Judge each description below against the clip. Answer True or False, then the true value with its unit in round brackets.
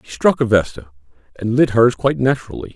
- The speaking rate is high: False (195 wpm)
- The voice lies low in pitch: True (120 Hz)